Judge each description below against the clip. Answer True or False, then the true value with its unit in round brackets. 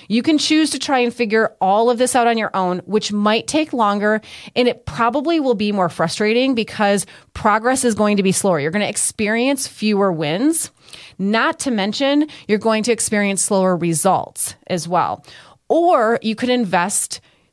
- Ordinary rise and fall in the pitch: True (4.0 semitones)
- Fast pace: False (180 wpm)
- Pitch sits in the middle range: False (220 Hz)